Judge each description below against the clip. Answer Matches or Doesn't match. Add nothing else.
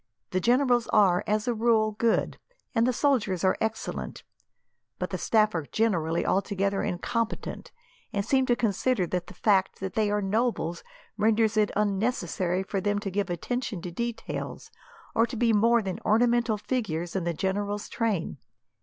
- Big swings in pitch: Doesn't match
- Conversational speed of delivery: Matches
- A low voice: Doesn't match